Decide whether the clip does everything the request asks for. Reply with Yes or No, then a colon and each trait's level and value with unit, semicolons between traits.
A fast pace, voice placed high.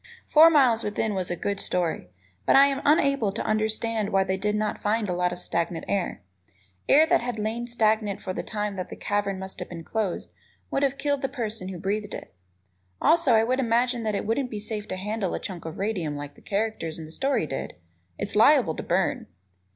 Yes: fast, 215 wpm; high, 210 Hz